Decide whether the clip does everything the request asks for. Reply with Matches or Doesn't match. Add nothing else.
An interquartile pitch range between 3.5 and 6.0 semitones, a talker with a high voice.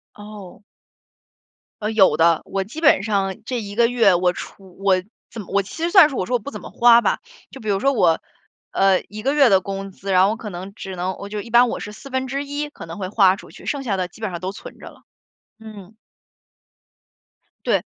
Matches